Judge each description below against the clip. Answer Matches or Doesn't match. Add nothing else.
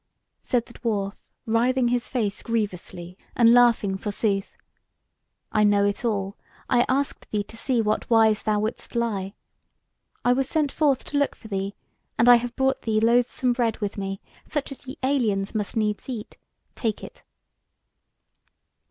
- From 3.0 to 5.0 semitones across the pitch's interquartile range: Matches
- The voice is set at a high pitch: Matches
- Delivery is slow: Doesn't match